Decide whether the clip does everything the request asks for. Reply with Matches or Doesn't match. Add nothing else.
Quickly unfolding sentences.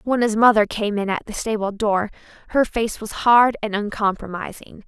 Doesn't match